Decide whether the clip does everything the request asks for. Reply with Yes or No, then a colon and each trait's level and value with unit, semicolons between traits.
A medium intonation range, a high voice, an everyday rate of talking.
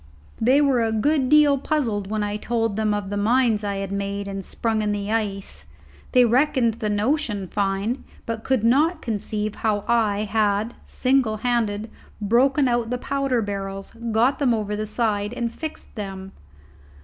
Yes: average, 3.3 semitones; high, 220 Hz; average, 170 wpm